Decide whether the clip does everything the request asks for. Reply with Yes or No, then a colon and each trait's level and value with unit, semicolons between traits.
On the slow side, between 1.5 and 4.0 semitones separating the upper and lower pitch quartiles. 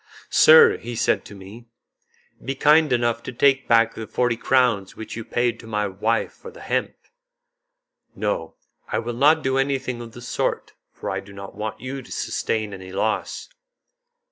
No: average, 175 wpm; average, 3.6 semitones